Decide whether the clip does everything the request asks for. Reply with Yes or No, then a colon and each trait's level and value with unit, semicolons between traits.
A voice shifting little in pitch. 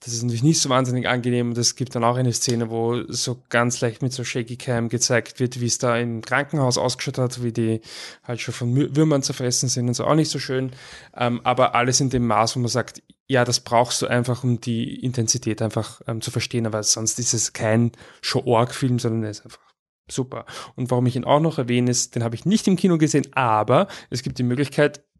Yes: narrow, 1.7 semitones